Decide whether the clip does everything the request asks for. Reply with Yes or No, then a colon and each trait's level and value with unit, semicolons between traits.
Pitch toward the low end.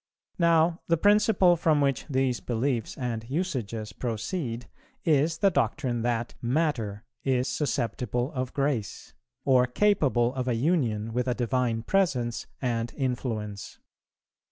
Yes: low, 125 Hz